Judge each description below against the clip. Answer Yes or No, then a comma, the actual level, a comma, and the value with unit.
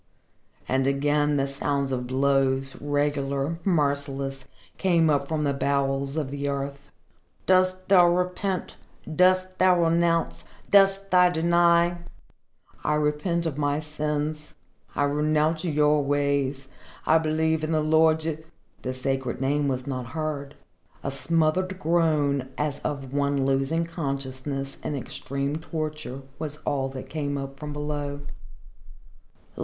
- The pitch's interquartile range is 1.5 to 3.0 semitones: Yes, average, 2.7 semitones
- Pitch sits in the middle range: Yes, medium, 150 Hz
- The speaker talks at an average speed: No, slow, 130 wpm